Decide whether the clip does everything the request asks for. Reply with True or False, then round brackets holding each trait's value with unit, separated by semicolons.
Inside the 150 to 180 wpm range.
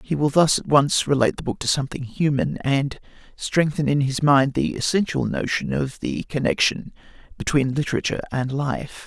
True (170 wpm)